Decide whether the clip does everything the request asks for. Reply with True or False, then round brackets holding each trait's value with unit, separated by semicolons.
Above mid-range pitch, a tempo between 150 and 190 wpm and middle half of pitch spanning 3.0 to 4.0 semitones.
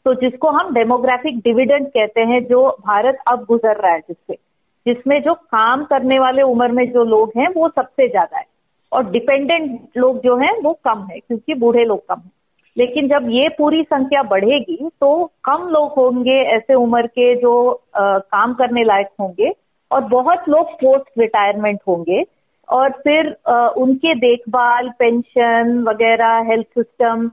True (250 Hz; 165 wpm; 3.3 semitones)